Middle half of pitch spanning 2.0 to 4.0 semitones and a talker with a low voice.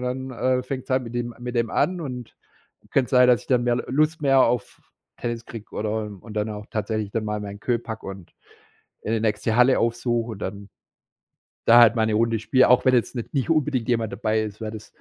Yes: narrow, 2.6 semitones; low, 115 Hz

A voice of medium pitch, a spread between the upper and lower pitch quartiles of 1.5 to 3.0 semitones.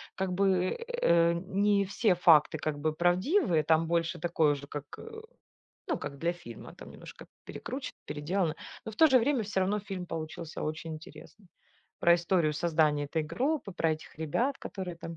No: medium, 170 Hz; average, 3.8 semitones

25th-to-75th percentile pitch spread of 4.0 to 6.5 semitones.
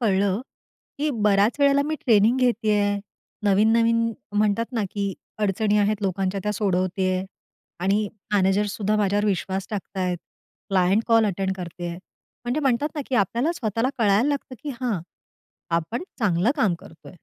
No: average, 3.1 semitones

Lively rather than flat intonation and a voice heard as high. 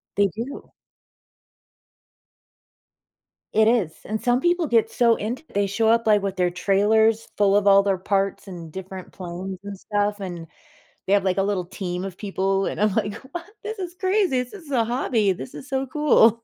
No: average, 4.0 semitones; high, 205 Hz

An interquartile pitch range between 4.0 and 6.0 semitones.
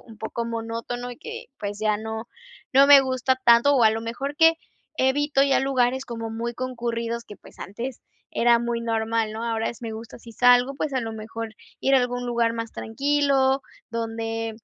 No: narrow, 2.6 semitones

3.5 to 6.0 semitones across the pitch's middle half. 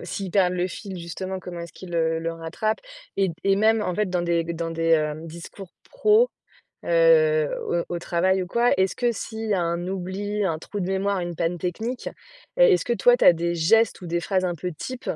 Yes: average, 4.1 semitones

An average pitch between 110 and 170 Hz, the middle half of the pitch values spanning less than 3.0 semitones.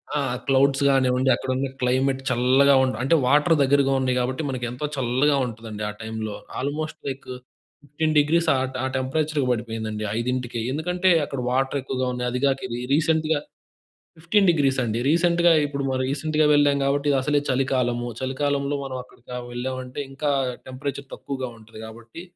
Yes: low, 135 Hz; narrow, 2.5 semitones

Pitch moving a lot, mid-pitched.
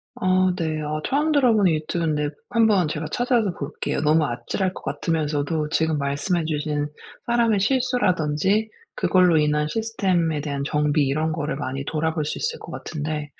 No: average, 4.5 semitones; medium, 160 Hz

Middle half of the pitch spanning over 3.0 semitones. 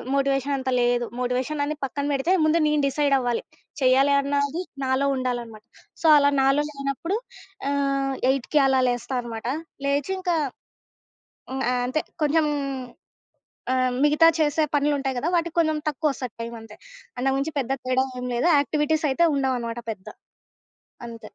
No: narrow, 2.6 semitones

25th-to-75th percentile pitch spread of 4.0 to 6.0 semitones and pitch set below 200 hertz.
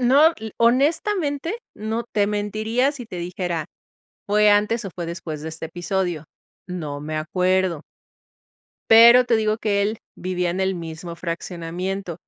Yes: average, 4.7 semitones; high, 190 Hz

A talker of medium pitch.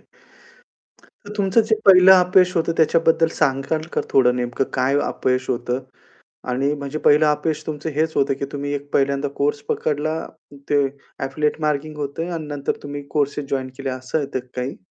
Yes: medium, 145 Hz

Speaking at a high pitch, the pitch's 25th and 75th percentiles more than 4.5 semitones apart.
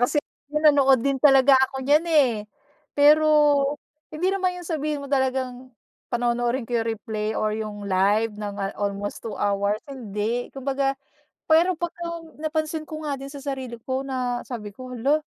Yes: very high, 265 Hz; average, 4.9 semitones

